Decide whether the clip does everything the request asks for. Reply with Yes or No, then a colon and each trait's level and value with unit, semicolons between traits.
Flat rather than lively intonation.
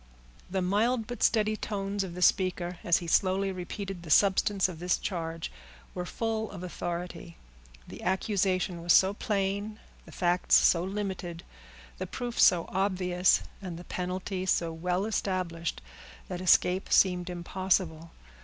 Yes: narrow, 2.1 semitones